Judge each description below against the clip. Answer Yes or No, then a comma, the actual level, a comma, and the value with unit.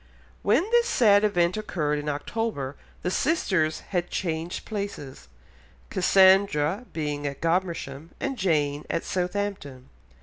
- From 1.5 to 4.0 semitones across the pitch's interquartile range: No, wide, 5.4 semitones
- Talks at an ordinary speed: No, slow, 125 wpm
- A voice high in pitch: No, medium, 175 Hz